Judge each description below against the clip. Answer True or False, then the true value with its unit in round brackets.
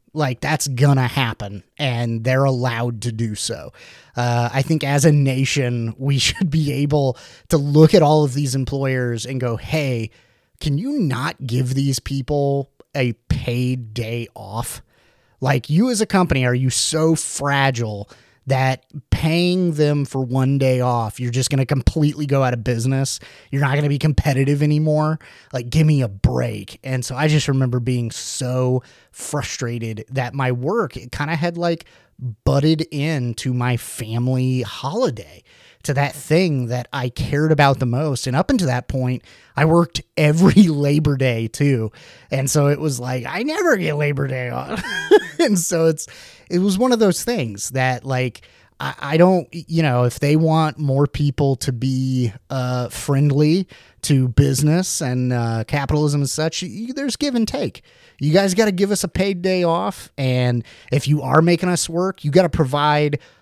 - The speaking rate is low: False (175 wpm)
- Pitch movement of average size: True (3.7 semitones)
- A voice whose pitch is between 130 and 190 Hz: True (140 Hz)